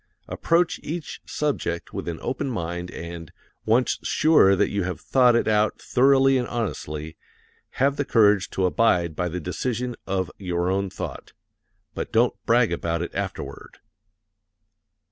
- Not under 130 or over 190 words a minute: Yes, average, 145 wpm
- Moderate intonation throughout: No, wide, 6.5 semitones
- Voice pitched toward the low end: Yes, low, 100 Hz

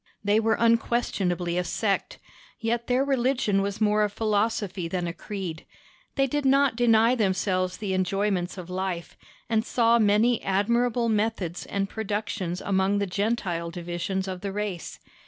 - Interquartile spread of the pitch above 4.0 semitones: No, average, 3.6 semitones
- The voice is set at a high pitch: Yes, high, 205 Hz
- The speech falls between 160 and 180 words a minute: No, average, 150 wpm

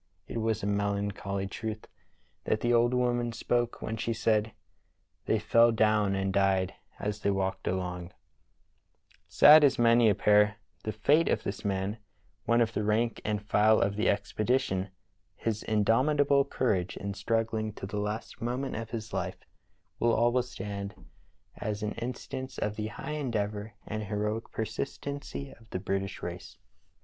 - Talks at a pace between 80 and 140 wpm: No, average, 160 wpm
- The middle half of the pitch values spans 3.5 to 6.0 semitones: No, narrow, 2.6 semitones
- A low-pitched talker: Yes, low, 110 Hz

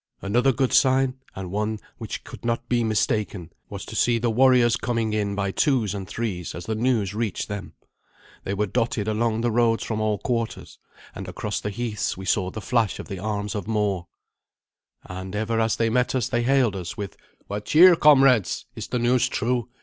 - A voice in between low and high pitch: No, low, 110 Hz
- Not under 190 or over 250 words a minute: Yes, average, 200 wpm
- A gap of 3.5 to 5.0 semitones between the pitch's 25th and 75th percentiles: No, average, 2.9 semitones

